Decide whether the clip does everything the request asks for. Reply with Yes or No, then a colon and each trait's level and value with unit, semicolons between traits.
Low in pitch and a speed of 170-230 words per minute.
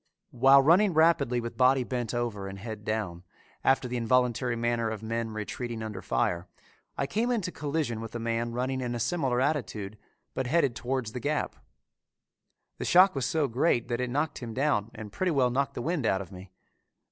Yes: low, 120 Hz; average, 195 wpm